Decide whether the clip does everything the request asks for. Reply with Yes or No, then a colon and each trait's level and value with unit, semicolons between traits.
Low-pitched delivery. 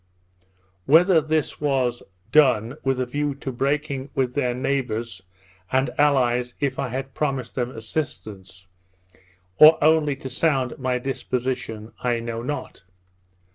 Yes: low, 130 Hz